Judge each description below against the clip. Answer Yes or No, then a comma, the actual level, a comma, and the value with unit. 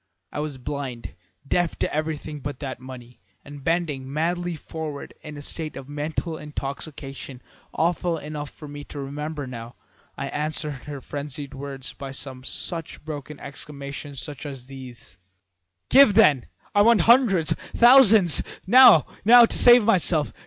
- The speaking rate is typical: Yes, average, 145 wpm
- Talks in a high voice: No, medium, 150 Hz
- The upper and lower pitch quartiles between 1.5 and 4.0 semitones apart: Yes, average, 3.3 semitones